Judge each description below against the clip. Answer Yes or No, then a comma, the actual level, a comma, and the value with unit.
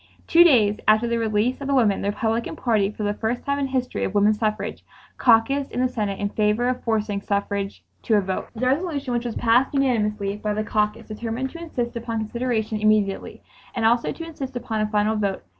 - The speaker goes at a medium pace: No, fast, 215 wpm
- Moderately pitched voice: No, high, 225 Hz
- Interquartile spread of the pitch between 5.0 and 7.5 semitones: No, average, 3.1 semitones